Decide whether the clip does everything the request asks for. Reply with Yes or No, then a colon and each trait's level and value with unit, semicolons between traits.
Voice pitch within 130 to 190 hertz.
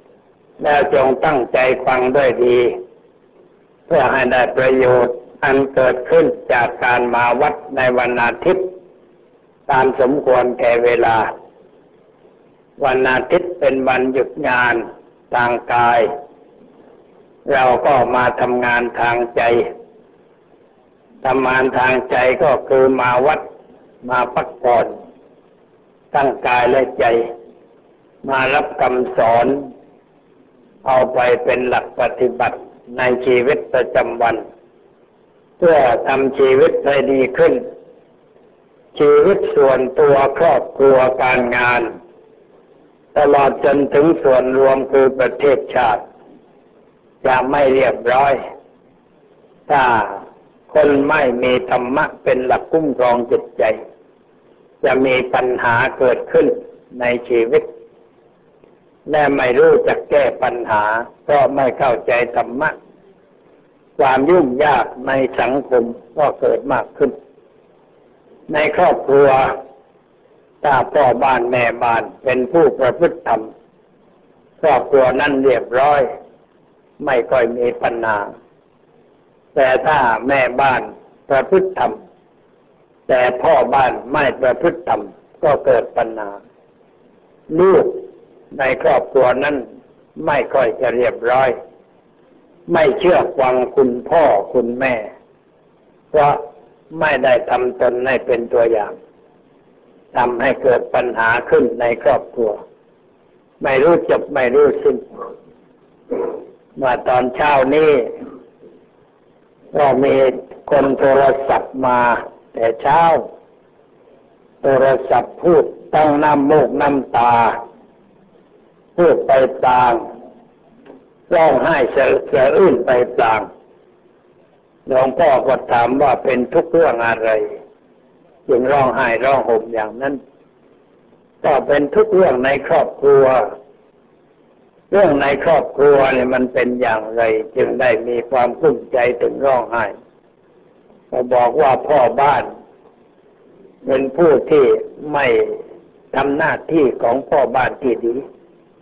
Yes: low, 135 Hz